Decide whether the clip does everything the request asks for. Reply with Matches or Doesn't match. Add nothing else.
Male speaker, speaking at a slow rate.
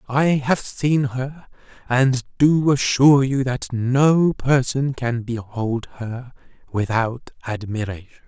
Matches